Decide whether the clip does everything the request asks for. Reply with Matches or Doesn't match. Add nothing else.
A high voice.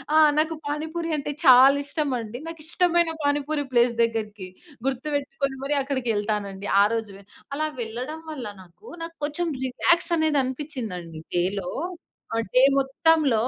Matches